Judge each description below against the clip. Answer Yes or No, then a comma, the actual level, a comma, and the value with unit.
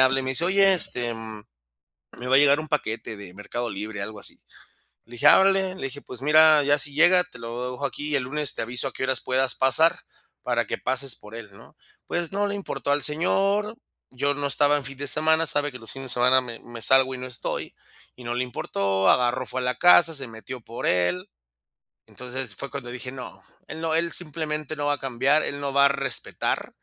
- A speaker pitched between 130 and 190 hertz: Yes, low, 135 Hz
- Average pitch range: Yes, average, 3.7 semitones